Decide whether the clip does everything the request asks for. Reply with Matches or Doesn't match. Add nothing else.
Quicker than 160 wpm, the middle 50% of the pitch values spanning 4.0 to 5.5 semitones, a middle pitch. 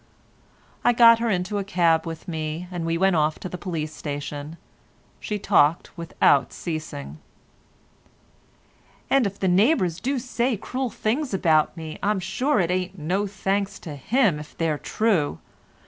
Doesn't match